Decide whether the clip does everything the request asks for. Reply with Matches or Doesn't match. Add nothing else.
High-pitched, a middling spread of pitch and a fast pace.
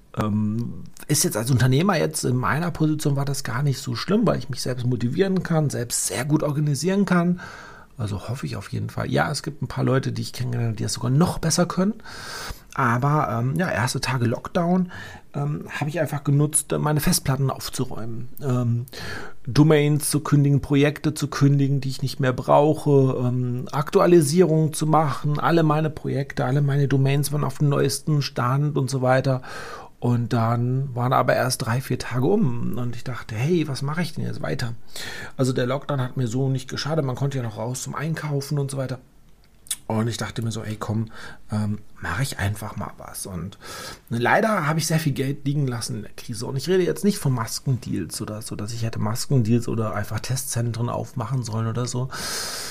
Doesn't match